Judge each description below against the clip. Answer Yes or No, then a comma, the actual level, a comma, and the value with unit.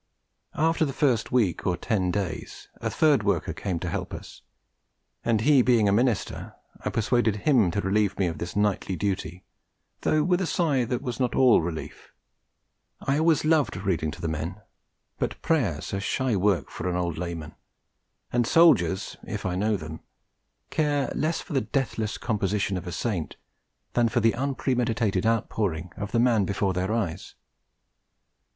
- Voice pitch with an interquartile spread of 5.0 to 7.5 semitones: Yes, wide, 5.6 semitones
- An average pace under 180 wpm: Yes, average, 170 wpm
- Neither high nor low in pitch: No, low, 105 Hz